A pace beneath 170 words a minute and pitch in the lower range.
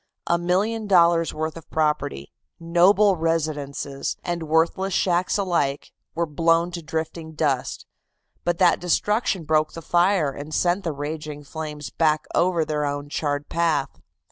No: average, 140 wpm; medium, 165 Hz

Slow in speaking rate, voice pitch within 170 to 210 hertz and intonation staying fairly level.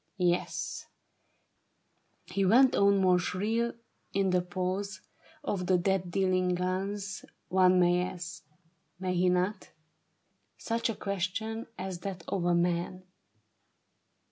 Yes: slow, 125 wpm; medium, 185 Hz; narrow, 1.8 semitones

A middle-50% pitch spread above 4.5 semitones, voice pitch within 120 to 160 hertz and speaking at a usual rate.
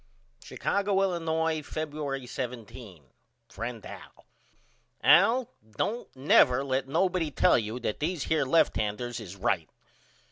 No: wide, 5.4 semitones; low, 135 Hz; slow, 110 wpm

